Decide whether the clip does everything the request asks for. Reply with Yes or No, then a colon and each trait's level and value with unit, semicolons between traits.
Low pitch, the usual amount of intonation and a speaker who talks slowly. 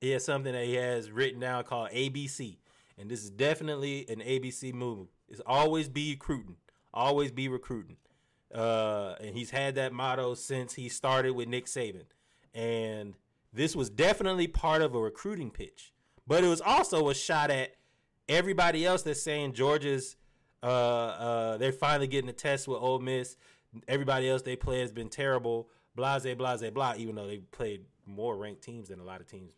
No: low, 130 Hz; average, 3.0 semitones; average, 185 wpm